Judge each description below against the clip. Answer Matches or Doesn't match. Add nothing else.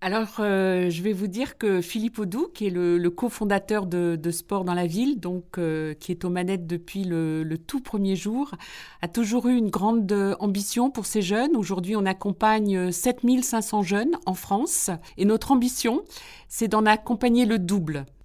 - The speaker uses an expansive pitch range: Doesn't match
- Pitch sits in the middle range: Doesn't match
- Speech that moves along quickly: Doesn't match